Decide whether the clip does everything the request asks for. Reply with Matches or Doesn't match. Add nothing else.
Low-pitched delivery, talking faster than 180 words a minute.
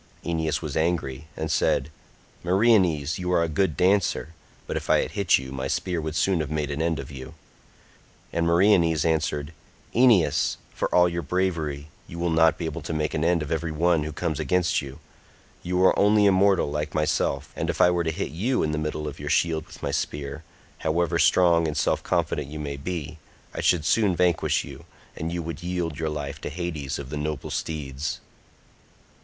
Matches